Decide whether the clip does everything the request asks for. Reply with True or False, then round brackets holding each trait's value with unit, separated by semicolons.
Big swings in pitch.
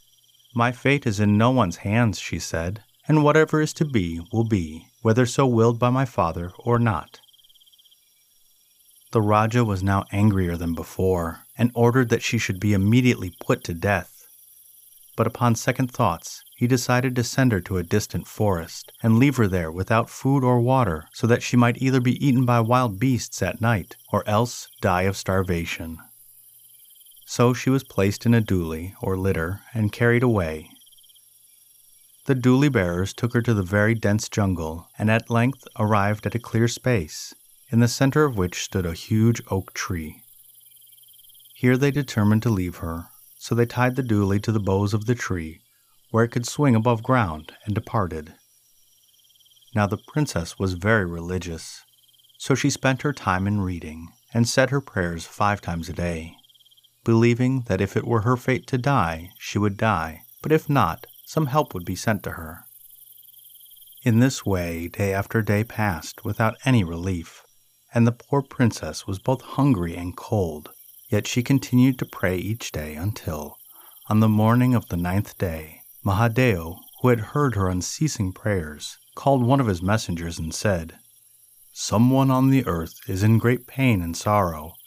False (4.6 semitones)